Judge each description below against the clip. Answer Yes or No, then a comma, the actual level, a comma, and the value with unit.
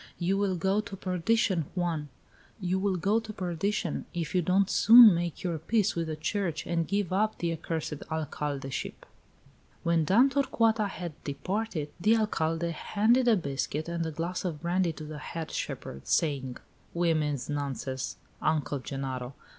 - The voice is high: No, medium, 170 Hz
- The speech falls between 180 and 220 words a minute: No, average, 155 wpm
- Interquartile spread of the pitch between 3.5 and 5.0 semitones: Yes, average, 4.5 semitones